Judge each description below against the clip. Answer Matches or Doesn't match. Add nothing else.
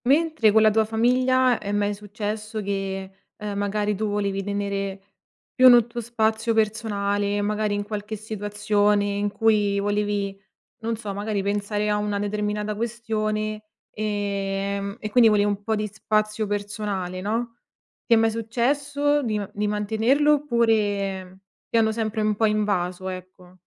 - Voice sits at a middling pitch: Doesn't match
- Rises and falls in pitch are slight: Matches